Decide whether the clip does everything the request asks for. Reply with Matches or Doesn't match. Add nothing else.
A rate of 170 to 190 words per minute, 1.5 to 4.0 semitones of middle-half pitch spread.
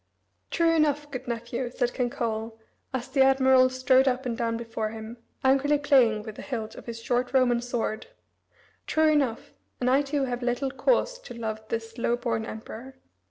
Matches